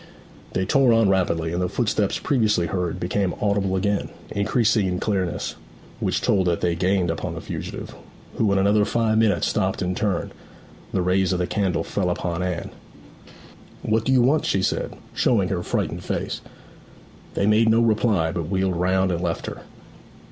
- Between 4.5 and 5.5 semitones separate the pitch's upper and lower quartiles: No, average, 3.1 semitones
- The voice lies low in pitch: Yes, very low, 95 Hz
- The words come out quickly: No, average, 175 wpm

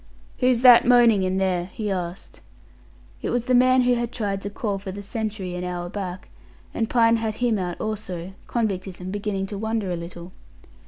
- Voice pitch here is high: Yes, high, 205 Hz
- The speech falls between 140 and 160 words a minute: No, average, 190 wpm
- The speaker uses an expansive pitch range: No, average, 3.7 semitones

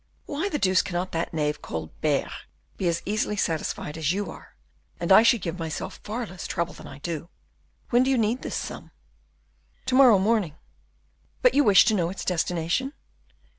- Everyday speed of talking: Yes, average, 180 wpm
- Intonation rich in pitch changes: Yes, wide, 5.7 semitones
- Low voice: No, medium, 185 Hz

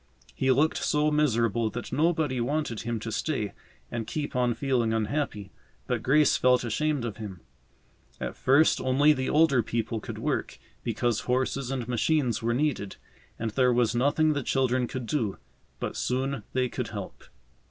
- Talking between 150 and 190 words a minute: Yes, average, 165 wpm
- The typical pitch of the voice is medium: No, low, 125 Hz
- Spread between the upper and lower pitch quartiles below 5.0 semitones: Yes, average, 3.7 semitones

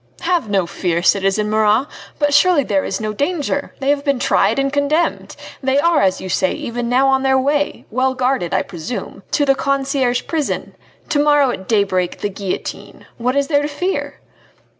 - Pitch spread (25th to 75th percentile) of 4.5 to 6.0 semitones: Yes, average, 5.3 semitones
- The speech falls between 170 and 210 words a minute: Yes, average, 185 wpm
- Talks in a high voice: Yes, very high, 265 Hz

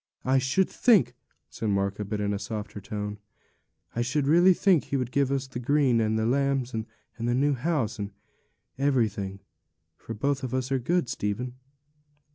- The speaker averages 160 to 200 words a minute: Yes, average, 175 wpm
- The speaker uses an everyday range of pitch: Yes, average, 4.5 semitones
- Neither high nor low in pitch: No, low, 125 Hz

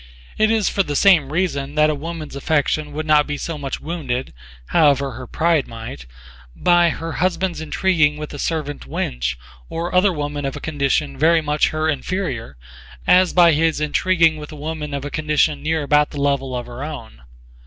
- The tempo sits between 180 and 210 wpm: Yes, average, 185 wpm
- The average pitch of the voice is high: No, medium, 150 Hz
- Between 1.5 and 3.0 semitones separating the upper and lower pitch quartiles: Yes, average, 2.7 semitones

